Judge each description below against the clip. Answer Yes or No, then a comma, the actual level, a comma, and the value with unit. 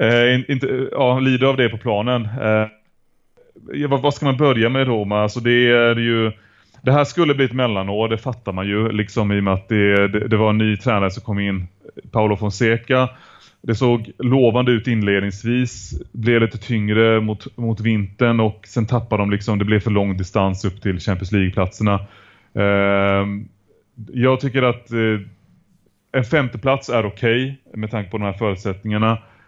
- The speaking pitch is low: Yes, low, 110 Hz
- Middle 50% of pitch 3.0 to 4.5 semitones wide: Yes, average, 3.3 semitones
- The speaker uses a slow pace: No, average, 185 wpm